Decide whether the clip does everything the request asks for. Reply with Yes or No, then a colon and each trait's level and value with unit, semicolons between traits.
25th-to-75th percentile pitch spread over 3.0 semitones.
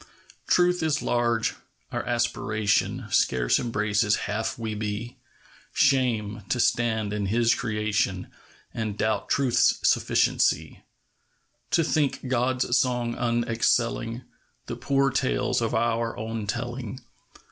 No: narrow, 2.6 semitones